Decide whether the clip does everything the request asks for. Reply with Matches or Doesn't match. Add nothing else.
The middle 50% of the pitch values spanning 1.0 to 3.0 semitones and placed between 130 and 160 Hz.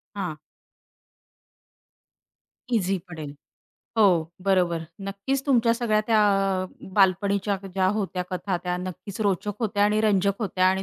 Doesn't match